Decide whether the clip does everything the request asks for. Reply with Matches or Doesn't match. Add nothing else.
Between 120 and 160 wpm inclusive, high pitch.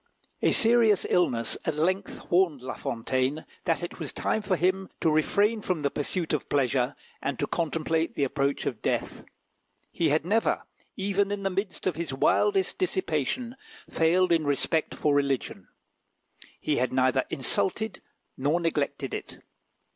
Doesn't match